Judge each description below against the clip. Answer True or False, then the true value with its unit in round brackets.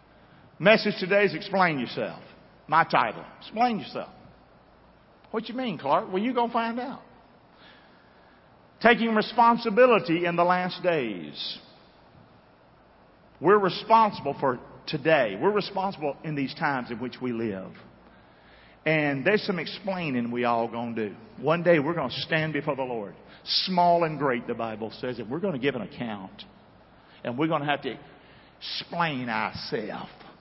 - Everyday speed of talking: True (150 wpm)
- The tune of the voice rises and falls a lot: True (7.2 semitones)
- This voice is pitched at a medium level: True (170 Hz)